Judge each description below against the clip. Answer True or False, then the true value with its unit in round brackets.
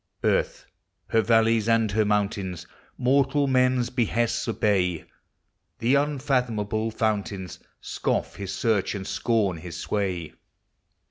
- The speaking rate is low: True (115 wpm)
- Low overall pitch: True (110 Hz)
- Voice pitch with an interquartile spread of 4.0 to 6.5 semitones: False (3.5 semitones)